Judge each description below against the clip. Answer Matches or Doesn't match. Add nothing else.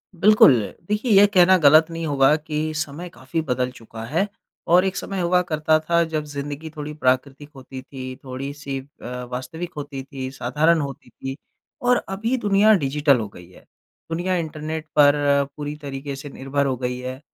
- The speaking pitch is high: Doesn't match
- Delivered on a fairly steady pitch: Doesn't match